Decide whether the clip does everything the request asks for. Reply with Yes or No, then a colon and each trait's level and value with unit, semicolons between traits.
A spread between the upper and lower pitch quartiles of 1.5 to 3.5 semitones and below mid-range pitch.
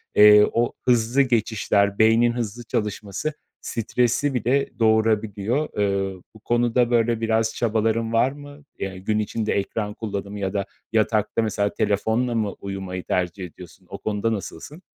Yes: narrow, 2.6 semitones; low, 110 Hz